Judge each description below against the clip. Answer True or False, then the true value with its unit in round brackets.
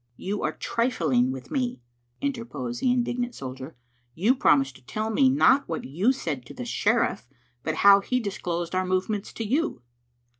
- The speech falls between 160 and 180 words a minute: True (175 wpm)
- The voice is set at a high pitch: True (200 Hz)